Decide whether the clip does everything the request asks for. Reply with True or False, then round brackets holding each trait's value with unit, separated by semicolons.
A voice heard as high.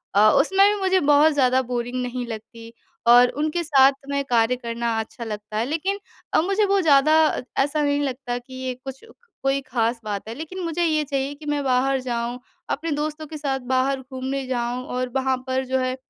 True (265 Hz)